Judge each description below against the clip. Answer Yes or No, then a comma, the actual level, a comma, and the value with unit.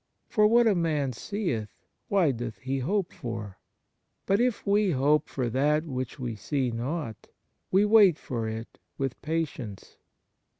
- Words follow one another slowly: No, average, 145 wpm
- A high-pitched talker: No, medium, 140 Hz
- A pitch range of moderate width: No, wide, 8.1 semitones